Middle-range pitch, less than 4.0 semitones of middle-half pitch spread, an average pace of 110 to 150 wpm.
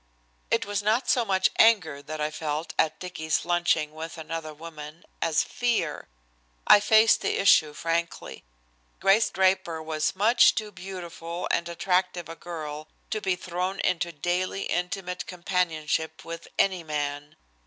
Yes: medium, 170 Hz; average, 3.2 semitones; average, 145 wpm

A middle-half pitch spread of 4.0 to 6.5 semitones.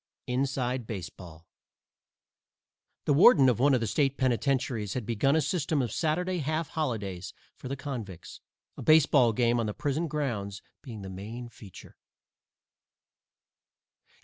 Yes: average, 5.1 semitones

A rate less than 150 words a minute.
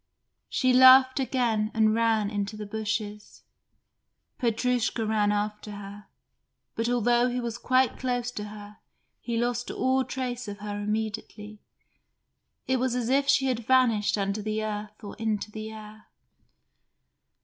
Yes: average, 140 wpm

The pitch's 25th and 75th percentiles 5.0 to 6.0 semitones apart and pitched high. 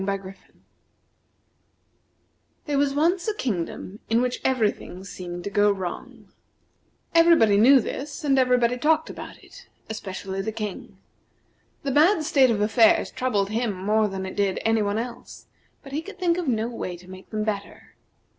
Yes: wide, 5.5 semitones; high, 225 Hz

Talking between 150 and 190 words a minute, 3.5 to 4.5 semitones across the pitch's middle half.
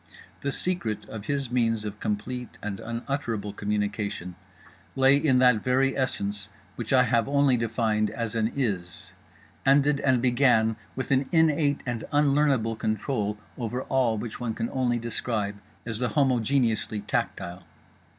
No: average, 140 wpm; average, 3.8 semitones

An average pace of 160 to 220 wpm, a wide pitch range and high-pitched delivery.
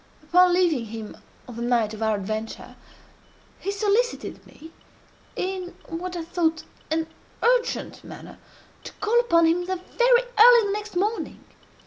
No: average, 140 wpm; wide, 5.8 semitones; very high, 355 Hz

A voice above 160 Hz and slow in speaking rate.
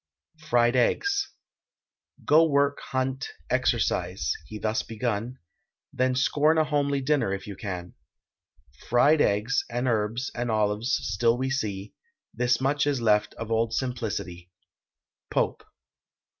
No: low, 120 Hz; slow, 125 wpm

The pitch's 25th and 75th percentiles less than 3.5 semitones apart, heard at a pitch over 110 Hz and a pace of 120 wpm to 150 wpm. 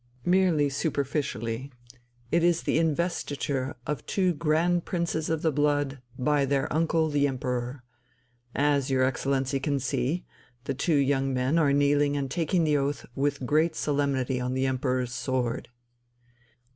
Yes: average, 2.9 semitones; medium, 140 Hz; average, 145 wpm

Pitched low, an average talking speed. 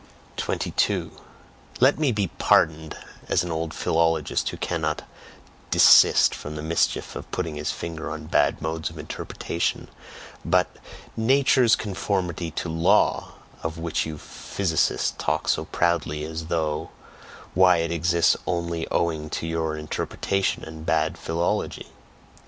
No: very low, 80 Hz; slow, 130 wpm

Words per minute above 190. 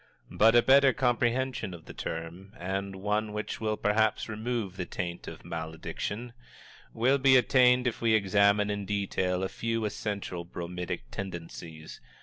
No: average, 145 wpm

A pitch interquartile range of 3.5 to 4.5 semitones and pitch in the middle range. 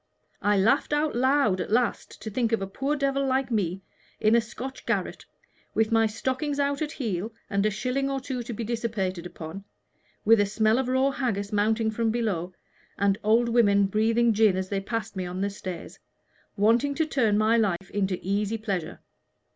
No: average, 4.0 semitones; high, 220 Hz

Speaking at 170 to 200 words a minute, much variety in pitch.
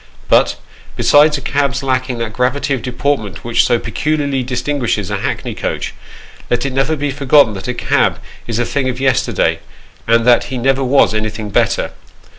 No: average, 180 wpm; average, 3.0 semitones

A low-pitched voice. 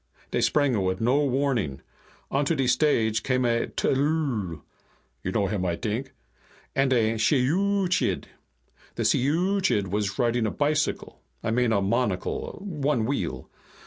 Yes: low, 125 Hz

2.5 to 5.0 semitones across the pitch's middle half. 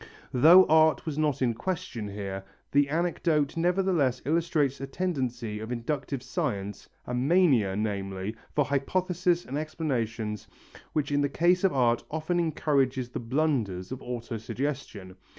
No: wide, 5.4 semitones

